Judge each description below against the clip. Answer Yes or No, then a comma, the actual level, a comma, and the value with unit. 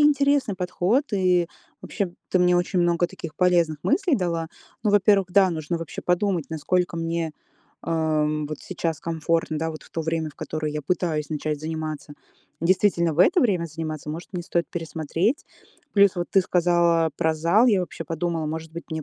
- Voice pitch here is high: No, medium, 170 Hz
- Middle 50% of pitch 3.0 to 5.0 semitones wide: No, narrow, 2.4 semitones